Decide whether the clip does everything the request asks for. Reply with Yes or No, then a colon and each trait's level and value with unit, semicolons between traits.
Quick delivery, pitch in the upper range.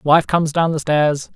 No: fast, 220 wpm; medium, 155 Hz